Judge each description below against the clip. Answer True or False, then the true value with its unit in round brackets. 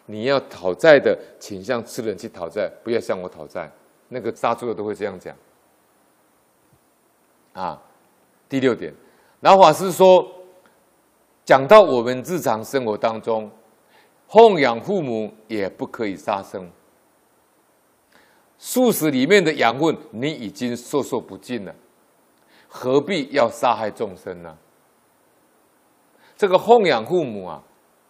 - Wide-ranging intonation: True (8.9 semitones)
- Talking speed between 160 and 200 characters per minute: True (185 characters per minute)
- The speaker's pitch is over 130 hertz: True (140 Hz)